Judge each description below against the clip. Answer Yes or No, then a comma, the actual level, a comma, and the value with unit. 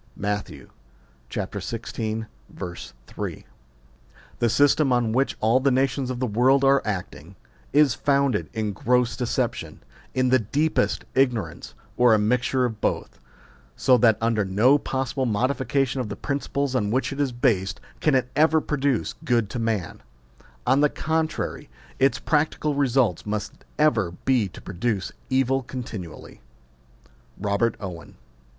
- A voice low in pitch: Yes, low, 125 Hz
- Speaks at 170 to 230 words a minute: No, slow, 135 wpm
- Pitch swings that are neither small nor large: Yes, average, 4.0 semitones